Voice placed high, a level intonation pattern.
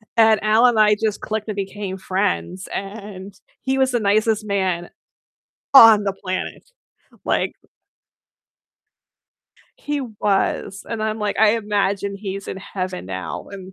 Yes: high, 205 Hz; narrow, 2.2 semitones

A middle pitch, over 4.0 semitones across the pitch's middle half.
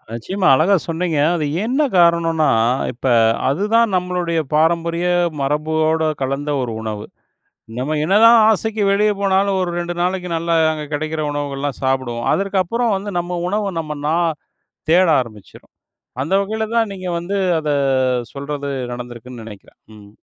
Yes: medium, 165 Hz; average, 5.2 semitones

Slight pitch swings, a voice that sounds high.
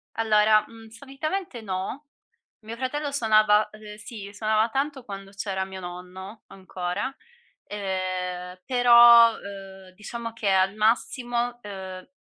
No: average, 3.7 semitones; high, 215 Hz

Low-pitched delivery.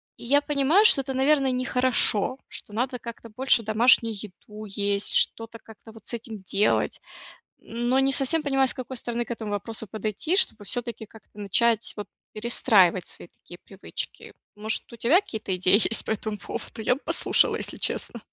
No: high, 230 Hz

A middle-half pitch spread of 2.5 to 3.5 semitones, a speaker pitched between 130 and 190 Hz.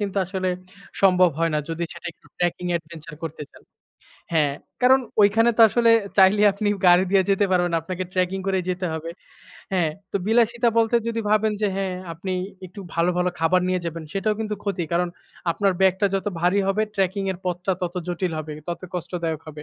Yes: average, 2.8 semitones; medium, 185 Hz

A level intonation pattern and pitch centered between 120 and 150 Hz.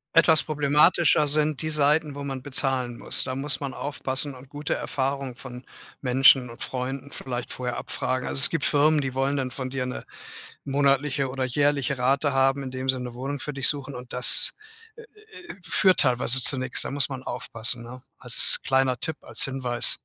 Yes: narrow, 2.1 semitones; low, 135 Hz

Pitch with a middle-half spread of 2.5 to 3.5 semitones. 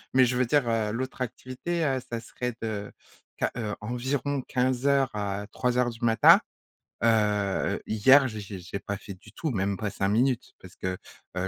No: average, 4.0 semitones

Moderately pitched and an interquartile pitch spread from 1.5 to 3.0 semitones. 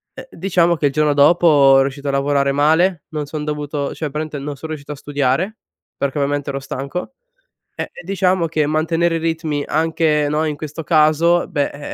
Yes: medium, 150 Hz; narrow, 2.5 semitones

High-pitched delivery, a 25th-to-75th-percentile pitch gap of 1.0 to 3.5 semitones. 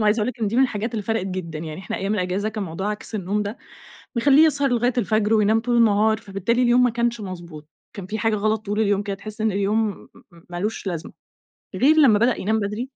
Yes: high, 215 Hz; average, 2.8 semitones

